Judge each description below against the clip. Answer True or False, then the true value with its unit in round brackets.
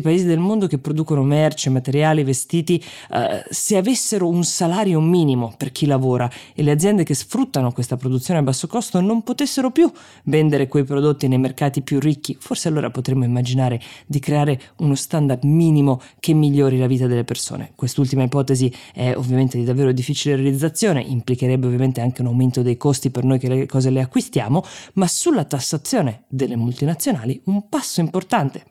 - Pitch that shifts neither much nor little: True (4.5 semitones)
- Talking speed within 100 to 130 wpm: False (170 wpm)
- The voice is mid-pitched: True (145 Hz)